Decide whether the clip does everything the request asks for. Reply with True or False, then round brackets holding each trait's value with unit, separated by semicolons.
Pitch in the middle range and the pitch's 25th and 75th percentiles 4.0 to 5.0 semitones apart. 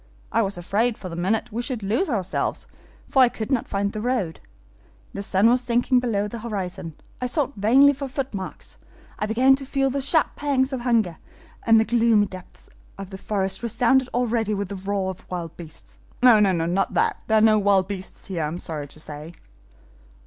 False (215 Hz; 4.5 semitones)